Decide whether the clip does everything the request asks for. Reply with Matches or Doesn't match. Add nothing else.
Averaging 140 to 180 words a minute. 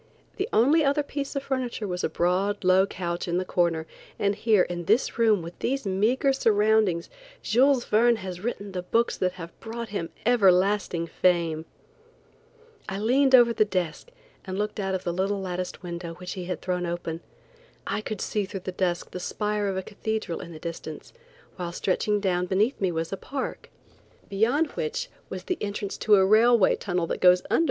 Doesn't match